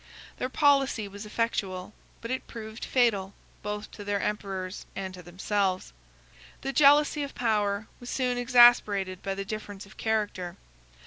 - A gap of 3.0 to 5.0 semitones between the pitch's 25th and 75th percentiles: Yes, average, 3.8 semitones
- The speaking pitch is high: Yes, high, 210 Hz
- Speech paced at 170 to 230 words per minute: No, average, 145 wpm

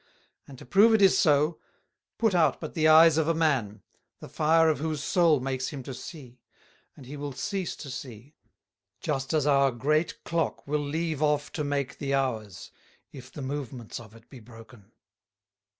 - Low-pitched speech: No, medium, 145 Hz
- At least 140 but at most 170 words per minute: No, average, 180 wpm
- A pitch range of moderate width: Yes, average, 3.6 semitones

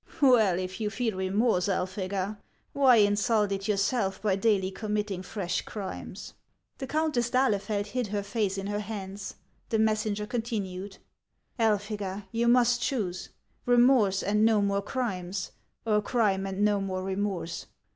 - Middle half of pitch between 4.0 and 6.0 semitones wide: No, average, 2.7 semitones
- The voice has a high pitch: Yes, high, 205 Hz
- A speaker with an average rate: Yes, average, 155 wpm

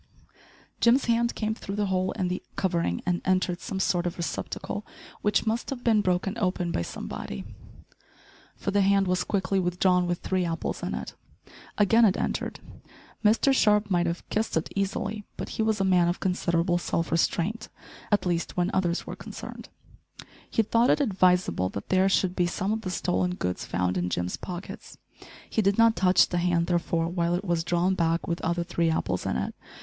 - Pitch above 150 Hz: Yes, medium, 185 Hz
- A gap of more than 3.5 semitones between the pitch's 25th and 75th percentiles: No, average, 2.8 semitones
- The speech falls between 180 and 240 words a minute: Yes, average, 190 wpm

